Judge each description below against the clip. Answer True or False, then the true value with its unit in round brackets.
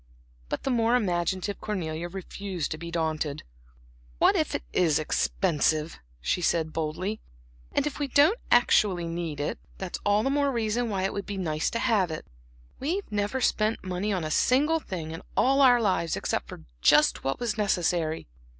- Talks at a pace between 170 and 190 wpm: True (175 wpm)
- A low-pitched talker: False (190 Hz)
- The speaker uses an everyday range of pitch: False (6.0 semitones)